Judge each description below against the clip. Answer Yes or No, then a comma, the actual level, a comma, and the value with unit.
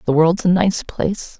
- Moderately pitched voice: Yes, medium, 175 Hz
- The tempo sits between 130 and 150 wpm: No, fast, 215 wpm